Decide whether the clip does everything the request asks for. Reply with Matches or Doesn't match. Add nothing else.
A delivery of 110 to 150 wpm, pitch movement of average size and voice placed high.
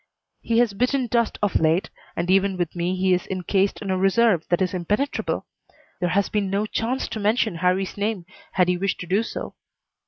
Doesn't match